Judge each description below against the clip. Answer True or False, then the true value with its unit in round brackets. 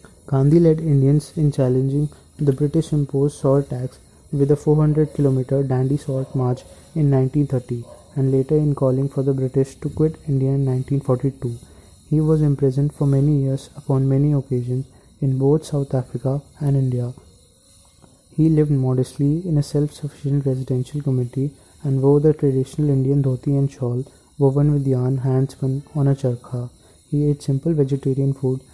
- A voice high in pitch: False (135 Hz)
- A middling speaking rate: True (150 wpm)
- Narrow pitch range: True (1.9 semitones)